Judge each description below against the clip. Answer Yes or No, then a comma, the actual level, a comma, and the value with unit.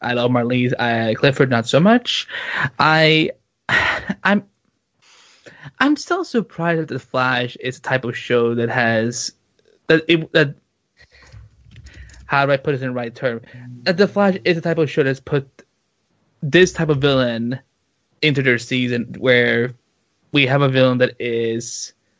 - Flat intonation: No, average, 4.7 semitones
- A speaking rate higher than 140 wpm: Yes, average, 160 wpm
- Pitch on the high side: No, low, 130 Hz